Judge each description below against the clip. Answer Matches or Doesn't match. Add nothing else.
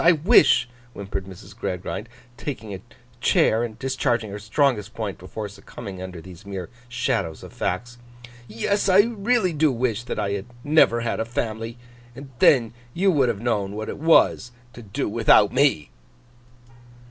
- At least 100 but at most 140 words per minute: Doesn't match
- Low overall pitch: Matches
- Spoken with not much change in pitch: Doesn't match